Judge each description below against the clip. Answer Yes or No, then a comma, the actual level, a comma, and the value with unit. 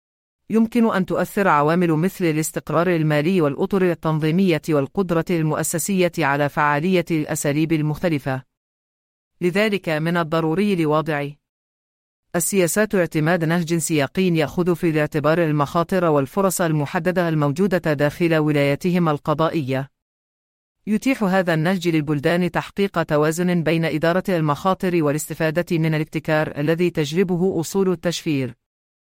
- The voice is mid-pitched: Yes, medium, 165 Hz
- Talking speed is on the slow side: Yes, slow, 100 wpm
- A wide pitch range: No, average, 3.0 semitones